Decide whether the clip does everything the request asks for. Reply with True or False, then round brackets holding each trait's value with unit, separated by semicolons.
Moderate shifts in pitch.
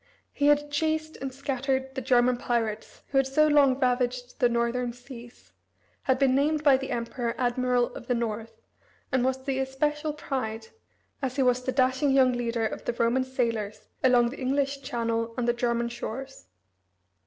False (2.2 semitones)